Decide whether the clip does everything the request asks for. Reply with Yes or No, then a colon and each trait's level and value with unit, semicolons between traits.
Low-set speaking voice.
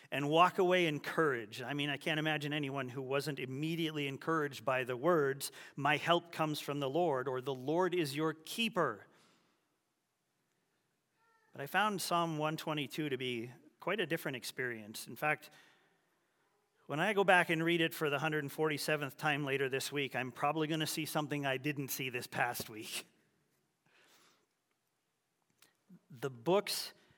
No: medium, 150 Hz